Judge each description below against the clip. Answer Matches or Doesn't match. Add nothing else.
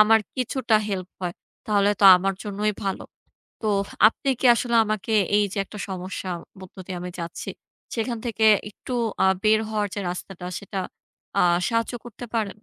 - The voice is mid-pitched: Doesn't match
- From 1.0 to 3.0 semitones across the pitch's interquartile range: Matches